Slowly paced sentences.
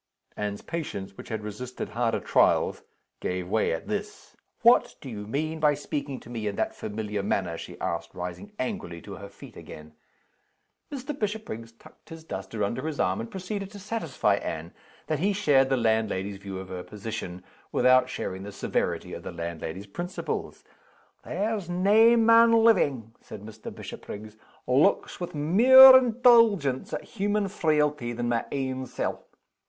No: average, 160 wpm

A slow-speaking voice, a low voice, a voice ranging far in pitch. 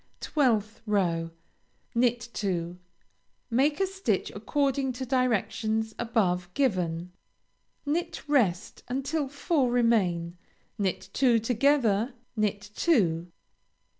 No: slow, 95 wpm; high, 230 Hz; wide, 6.0 semitones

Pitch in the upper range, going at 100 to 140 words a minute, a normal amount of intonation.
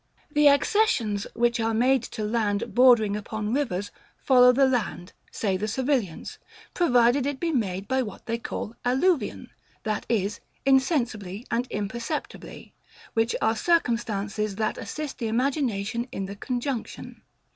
Yes: high, 235 Hz; slow, 135 wpm; average, 3.8 semitones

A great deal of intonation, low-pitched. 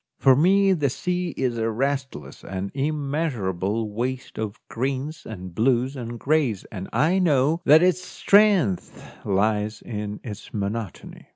Yes: wide, 6.4 semitones; low, 130 Hz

